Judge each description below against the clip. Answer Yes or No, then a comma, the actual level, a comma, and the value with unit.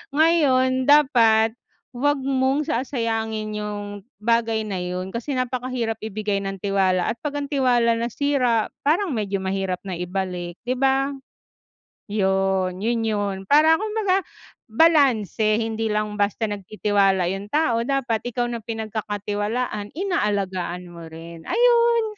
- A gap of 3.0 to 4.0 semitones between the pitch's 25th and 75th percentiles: No, average, 4.9 semitones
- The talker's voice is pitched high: Yes, high, 220 Hz